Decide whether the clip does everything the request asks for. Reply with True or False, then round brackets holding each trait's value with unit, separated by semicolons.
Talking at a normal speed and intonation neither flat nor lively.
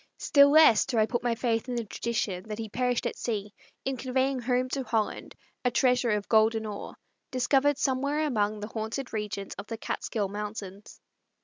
True (185 wpm; 3.4 semitones)